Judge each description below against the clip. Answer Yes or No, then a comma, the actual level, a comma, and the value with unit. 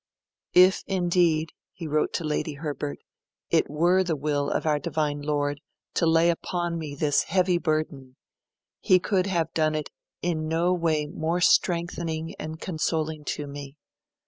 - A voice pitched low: No, medium, 160 Hz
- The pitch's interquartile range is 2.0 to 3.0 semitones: Yes, narrow, 2.5 semitones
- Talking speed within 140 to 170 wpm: Yes, average, 150 wpm